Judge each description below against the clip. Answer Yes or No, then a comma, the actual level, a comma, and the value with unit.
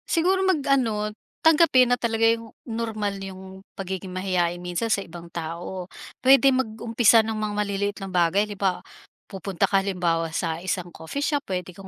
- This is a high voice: Yes, high, 200 Hz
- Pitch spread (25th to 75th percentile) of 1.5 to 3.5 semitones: No, average, 4.0 semitones